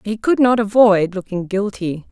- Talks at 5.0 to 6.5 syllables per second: No, 4.5 syllables/s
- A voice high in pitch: Yes, high, 205 Hz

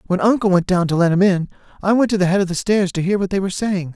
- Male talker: Yes, male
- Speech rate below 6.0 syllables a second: No, 7.0 syllables/s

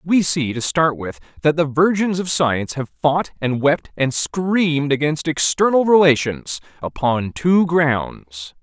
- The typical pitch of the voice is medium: Yes, medium, 150 Hz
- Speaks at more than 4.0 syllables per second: No, 3.9 syllables/s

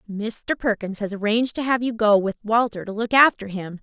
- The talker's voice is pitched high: Yes, high, 220 Hz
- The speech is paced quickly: Yes, fast, 220 wpm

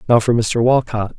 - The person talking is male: Yes, male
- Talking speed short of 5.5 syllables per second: Yes, 5.0 syllables/s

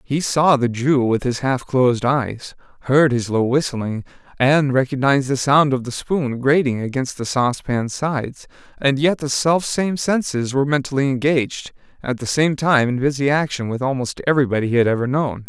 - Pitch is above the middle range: No, low, 135 Hz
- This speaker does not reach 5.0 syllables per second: No, 5.1 syllables/s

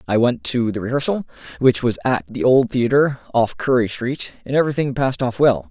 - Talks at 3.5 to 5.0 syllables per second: No, 5.5 syllables/s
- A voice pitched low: Yes, low, 125 Hz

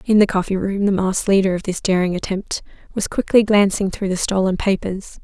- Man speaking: No, female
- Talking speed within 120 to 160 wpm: No, fast, 205 wpm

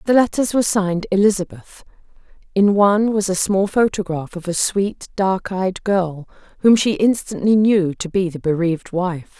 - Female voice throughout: Yes, female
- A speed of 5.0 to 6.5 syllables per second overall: No, 4.8 syllables/s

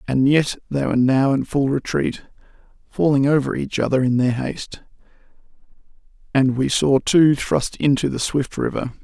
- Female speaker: No, male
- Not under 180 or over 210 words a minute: No, average, 160 wpm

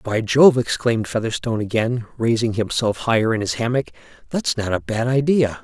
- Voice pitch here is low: Yes, low, 115 Hz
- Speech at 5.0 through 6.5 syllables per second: Yes, 5.4 syllables/s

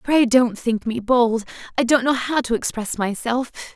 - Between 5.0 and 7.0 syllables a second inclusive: No, 4.5 syllables/s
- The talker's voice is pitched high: Yes, high, 240 Hz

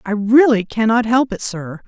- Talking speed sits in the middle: Yes, average, 190 wpm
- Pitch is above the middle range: Yes, high, 225 Hz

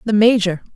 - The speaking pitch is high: Yes, high, 205 Hz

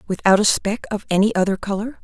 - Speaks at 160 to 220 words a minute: Yes, fast, 205 wpm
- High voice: Yes, high, 205 Hz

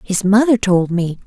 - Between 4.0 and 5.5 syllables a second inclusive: Yes, 4.5 syllables/s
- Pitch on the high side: Yes, high, 200 Hz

